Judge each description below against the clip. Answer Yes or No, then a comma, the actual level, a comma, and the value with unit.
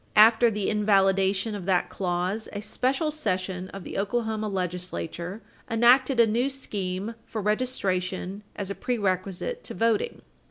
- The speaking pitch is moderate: No, high, 205 Hz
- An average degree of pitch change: Yes, average, 3.7 semitones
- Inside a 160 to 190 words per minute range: No, slow, 135 wpm